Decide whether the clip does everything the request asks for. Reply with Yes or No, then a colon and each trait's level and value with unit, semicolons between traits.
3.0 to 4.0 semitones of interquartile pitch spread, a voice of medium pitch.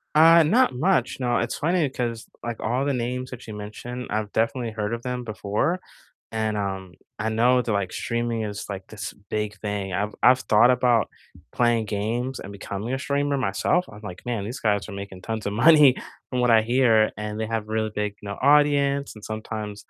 No: average, 3.3 semitones; low, 115 Hz